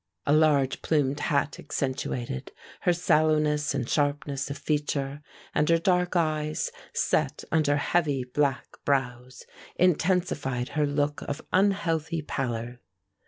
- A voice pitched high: No, medium, 145 Hz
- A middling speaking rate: No, slow, 120 wpm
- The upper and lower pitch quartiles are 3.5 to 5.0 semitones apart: No, narrow, 2.4 semitones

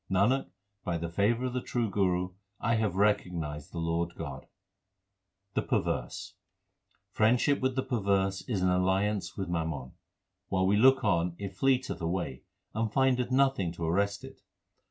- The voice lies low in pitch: Yes, very low, 95 Hz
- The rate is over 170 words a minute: No, average, 155 wpm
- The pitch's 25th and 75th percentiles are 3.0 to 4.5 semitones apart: No, average, 5.1 semitones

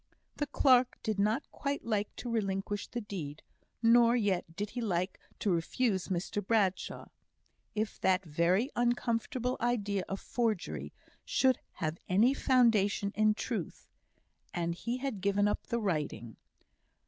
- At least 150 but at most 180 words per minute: No, slow, 135 wpm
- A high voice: Yes, high, 205 Hz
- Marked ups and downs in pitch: No, average, 4.1 semitones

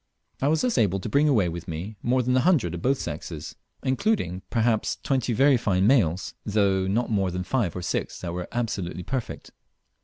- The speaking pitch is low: Yes, low, 105 Hz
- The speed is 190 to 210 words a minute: Yes, average, 195 wpm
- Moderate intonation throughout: No, wide, 6.2 semitones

